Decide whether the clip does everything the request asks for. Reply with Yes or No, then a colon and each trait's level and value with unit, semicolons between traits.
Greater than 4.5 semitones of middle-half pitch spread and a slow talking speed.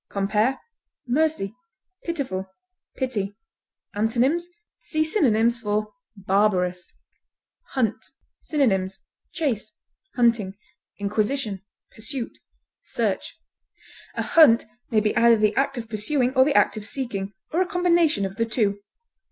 Yes: average, 5.0 semitones; slow, 110 wpm